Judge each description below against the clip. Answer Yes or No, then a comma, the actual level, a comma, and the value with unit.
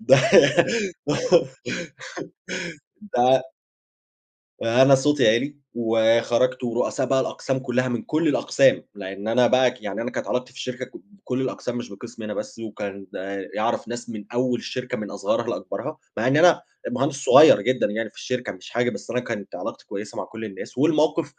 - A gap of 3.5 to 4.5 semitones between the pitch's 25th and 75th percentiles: No, average, 2.8 semitones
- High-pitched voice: No, low, 125 Hz